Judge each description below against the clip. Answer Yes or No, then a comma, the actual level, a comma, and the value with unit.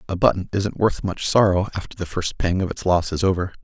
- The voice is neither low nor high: No, very low, 95 Hz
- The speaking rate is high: Yes, fast, 245 wpm